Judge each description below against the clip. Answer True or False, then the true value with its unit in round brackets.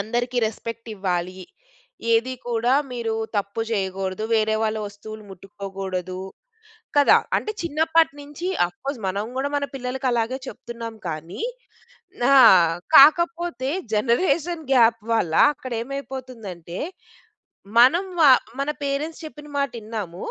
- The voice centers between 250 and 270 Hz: False (235 Hz)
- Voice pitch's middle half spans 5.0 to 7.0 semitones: True (5.6 semitones)